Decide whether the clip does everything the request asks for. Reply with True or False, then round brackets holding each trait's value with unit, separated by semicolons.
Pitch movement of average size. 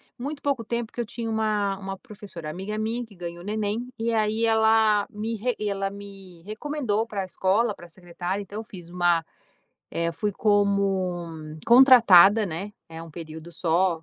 True (3.9 semitones)